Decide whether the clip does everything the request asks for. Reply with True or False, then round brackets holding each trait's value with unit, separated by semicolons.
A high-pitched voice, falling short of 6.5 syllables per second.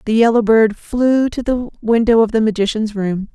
True (225 Hz; 4.7 syllables/s)